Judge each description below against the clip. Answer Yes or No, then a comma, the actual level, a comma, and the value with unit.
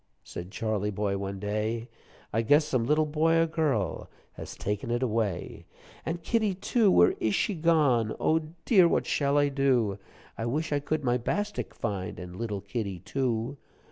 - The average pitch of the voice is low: Yes, low, 120 Hz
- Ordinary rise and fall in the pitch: No, wide, 6.9 semitones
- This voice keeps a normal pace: Yes, average, 175 wpm